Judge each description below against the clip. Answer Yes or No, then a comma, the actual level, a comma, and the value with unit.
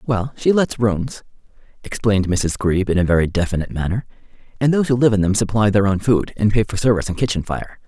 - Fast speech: Yes, fast, 220 wpm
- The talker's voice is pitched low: Yes, low, 105 Hz